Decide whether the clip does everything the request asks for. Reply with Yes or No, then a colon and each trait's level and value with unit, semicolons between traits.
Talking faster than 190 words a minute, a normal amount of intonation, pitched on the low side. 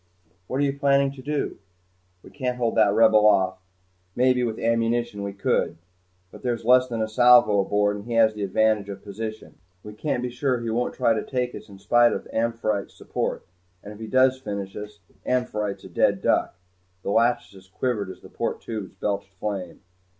Yes: average, 200 wpm; average, 3.2 semitones; low, 110 Hz